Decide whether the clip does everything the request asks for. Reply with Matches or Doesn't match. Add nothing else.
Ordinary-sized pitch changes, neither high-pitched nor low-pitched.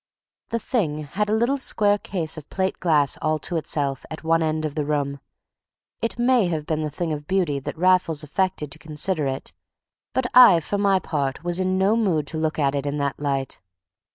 Matches